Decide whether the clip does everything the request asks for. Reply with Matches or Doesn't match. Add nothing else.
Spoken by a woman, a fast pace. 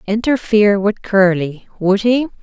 Doesn't match